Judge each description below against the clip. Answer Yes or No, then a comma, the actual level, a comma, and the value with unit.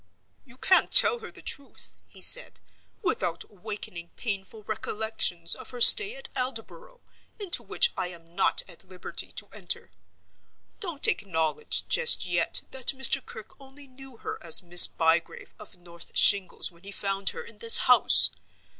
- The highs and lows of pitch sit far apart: Yes, wide, 7.7 semitones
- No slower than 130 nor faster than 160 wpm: Yes, average, 155 wpm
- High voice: Yes, high, 220 Hz